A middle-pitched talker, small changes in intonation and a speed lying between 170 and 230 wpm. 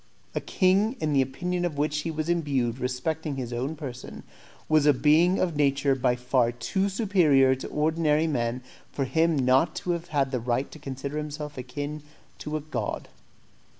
No: medium, 150 Hz; average, 3.5 semitones; average, 180 wpm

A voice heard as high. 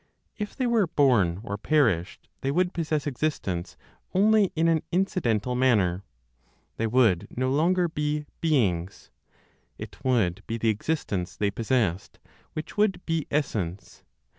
No: low, 130 Hz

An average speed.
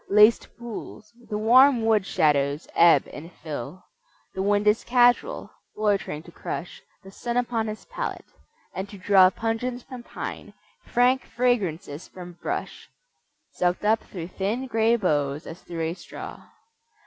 Yes: average, 145 wpm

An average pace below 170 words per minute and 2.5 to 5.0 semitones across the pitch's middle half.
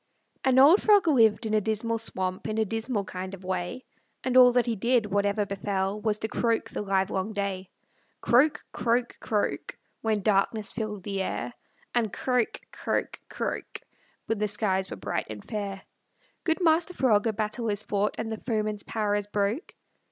No: average, 175 wpm; average, 2.8 semitones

